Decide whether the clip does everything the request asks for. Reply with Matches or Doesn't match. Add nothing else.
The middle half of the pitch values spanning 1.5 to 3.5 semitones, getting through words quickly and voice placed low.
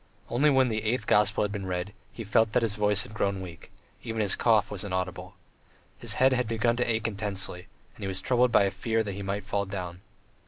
Matches